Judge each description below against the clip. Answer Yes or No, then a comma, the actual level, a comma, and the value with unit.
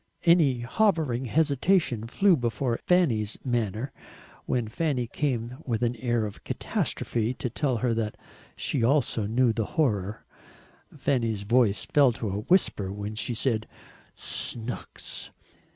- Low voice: Yes, low, 120 Hz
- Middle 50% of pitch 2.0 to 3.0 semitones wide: No, average, 3.9 semitones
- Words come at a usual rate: No, slow, 125 wpm